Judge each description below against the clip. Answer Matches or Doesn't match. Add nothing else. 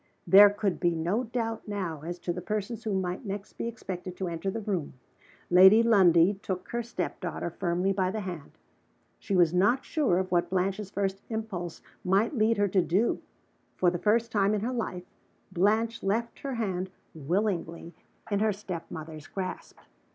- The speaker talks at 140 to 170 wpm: Doesn't match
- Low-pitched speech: Doesn't match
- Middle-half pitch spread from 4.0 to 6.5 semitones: Doesn't match